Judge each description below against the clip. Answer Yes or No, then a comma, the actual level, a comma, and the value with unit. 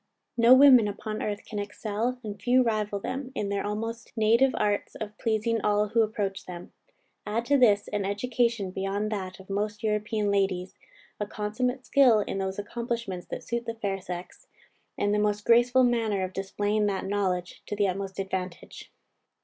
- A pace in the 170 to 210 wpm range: Yes, average, 175 wpm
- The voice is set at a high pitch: Yes, high, 210 Hz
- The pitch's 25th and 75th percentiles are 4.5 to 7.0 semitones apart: No, narrow, 2.6 semitones